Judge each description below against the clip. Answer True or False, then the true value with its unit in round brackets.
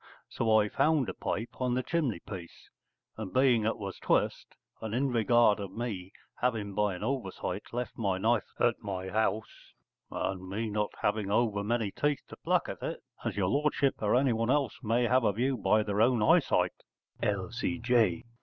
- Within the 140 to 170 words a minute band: False (180 wpm)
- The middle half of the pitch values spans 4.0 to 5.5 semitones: False (3.3 semitones)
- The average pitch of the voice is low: True (110 Hz)